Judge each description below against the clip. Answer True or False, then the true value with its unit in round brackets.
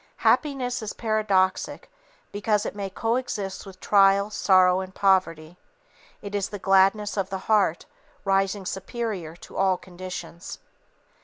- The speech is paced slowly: True (130 wpm)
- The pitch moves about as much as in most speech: False (2.0 semitones)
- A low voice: False (195 Hz)